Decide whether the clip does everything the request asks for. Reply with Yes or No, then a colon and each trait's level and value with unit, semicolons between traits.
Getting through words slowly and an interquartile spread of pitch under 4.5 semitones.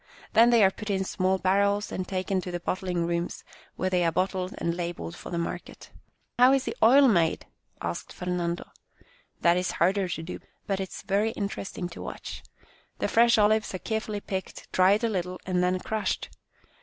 No: average, 200 wpm; narrow, 2.6 semitones